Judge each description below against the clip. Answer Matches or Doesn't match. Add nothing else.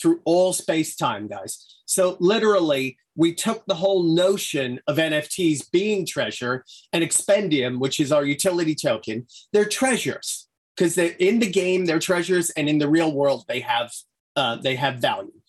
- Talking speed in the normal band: Matches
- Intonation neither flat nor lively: Matches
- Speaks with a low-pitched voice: Doesn't match